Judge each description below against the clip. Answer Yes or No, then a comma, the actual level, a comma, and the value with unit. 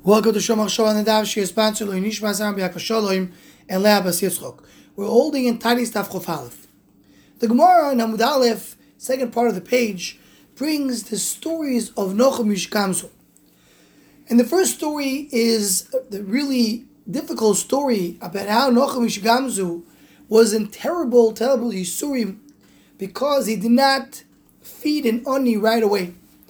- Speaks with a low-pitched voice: No, high, 225 Hz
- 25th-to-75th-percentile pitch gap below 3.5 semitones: No, average, 4.2 semitones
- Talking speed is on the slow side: Yes, slow, 130 wpm